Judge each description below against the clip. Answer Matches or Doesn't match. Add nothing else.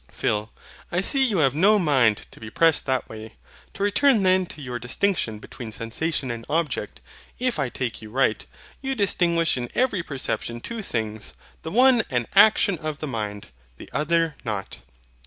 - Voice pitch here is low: Doesn't match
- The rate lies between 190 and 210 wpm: Doesn't match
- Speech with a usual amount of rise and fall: Doesn't match